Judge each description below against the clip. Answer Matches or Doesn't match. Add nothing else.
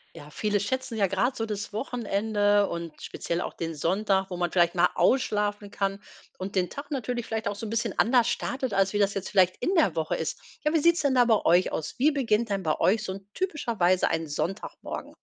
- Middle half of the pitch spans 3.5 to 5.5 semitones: Matches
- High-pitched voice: Matches